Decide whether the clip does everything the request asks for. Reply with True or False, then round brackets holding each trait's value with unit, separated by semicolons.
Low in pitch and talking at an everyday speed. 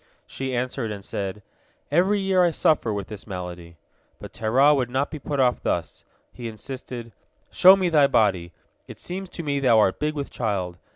True (125 Hz; 185 wpm)